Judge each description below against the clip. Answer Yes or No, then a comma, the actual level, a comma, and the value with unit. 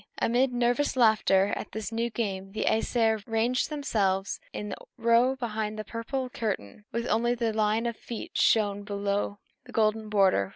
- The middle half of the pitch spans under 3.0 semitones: Yes, narrow, 2.5 semitones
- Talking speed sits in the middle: Yes, average, 165 wpm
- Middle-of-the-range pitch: No, high, 220 Hz